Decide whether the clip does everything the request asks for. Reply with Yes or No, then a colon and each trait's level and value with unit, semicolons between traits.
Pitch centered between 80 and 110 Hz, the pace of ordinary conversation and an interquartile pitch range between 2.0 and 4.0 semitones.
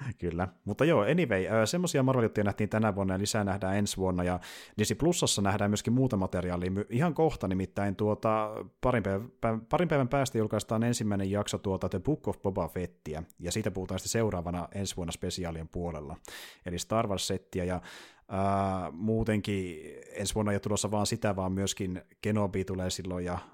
No: low, 100 Hz; fast, 170 wpm; average, 2.8 semitones